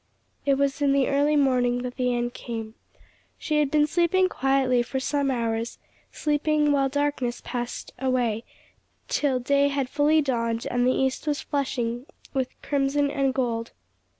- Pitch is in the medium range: No, very high, 270 Hz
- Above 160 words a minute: No, average, 155 wpm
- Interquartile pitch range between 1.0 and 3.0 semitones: Yes, average, 2.7 semitones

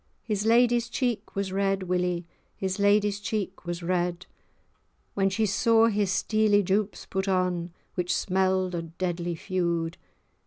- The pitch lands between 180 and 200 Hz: Yes, high, 190 Hz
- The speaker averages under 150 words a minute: Yes, average, 140 wpm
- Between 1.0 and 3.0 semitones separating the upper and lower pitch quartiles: Yes, narrow, 2.6 semitones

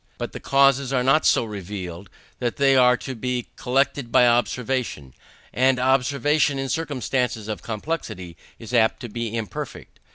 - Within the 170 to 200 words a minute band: No, average, 150 wpm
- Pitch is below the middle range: Yes, low, 125 Hz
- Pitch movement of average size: Yes, average, 3.4 semitones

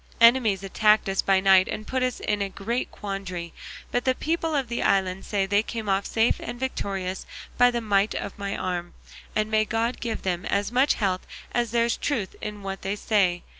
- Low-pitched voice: No, high, 210 Hz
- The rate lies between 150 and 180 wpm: No, fast, 205 wpm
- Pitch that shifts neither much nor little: Yes, average, 3.5 semitones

